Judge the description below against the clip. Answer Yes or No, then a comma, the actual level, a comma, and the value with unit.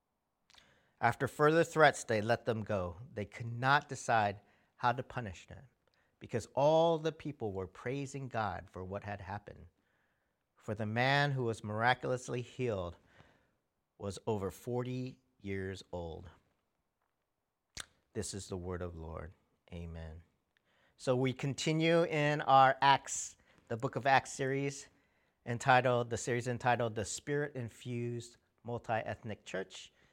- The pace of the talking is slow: Yes, slow, 130 wpm